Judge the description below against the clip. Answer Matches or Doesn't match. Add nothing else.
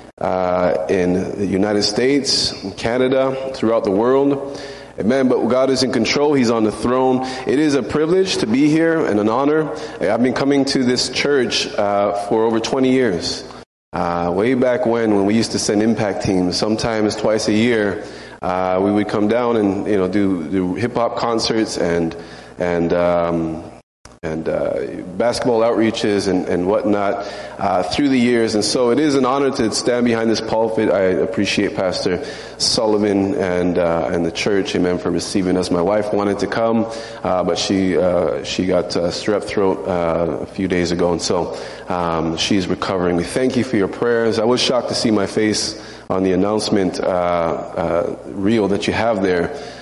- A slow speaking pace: Doesn't match